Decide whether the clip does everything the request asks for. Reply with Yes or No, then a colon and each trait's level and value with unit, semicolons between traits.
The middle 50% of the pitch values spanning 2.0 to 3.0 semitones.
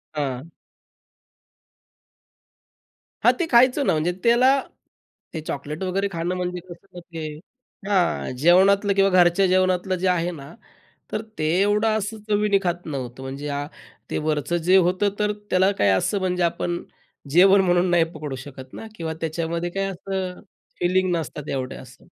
No: average, 3.5 semitones